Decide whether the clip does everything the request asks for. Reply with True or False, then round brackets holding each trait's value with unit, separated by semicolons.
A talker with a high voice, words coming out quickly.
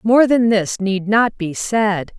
False (210 Hz; 190 wpm)